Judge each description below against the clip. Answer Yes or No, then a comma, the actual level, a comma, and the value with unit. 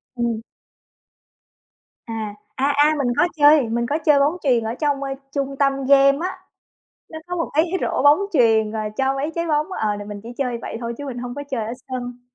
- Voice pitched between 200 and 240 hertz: No, very high, 270 Hz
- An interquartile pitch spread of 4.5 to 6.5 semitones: No, average, 3.8 semitones